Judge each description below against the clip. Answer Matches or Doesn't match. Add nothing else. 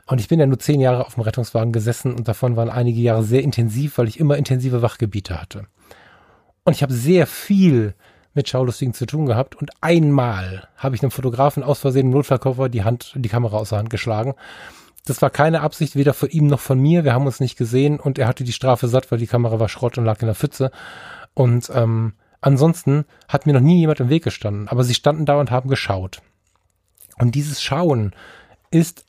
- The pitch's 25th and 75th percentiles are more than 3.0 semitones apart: Matches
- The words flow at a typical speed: Doesn't match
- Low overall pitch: Matches